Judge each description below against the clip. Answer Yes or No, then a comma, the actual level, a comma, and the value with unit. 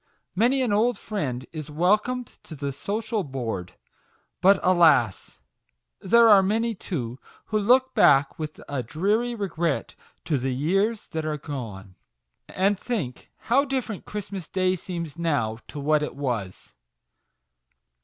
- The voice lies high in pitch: No, medium, 175 Hz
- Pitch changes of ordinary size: No, wide, 7.1 semitones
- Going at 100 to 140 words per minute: Yes, slow, 135 wpm